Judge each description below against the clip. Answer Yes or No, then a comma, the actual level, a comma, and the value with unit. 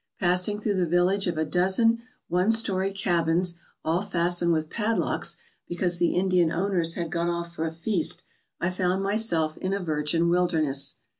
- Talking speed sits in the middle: Yes, average, 170 wpm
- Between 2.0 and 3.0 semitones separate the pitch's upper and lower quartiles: Yes, narrow, 2.4 semitones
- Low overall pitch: No, medium, 175 Hz